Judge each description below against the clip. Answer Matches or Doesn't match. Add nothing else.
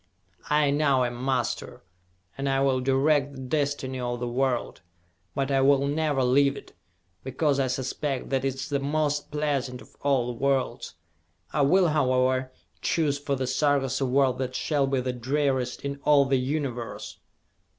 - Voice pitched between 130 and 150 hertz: Matches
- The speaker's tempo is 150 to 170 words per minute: Matches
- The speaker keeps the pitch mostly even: Matches